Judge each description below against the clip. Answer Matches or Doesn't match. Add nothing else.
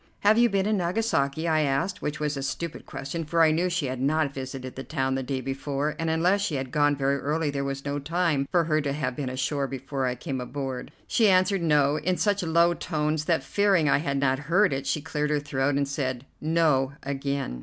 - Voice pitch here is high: Doesn't match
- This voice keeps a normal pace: Doesn't match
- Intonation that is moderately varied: Matches